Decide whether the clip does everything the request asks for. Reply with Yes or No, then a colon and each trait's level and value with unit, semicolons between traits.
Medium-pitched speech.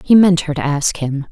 Yes: medium, 160 Hz